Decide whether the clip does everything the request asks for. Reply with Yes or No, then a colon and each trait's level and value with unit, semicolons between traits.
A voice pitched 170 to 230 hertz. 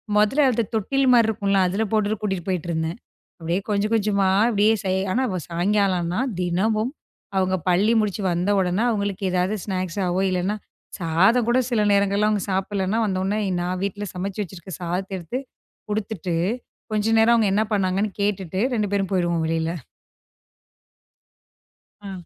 Yes: high, 195 Hz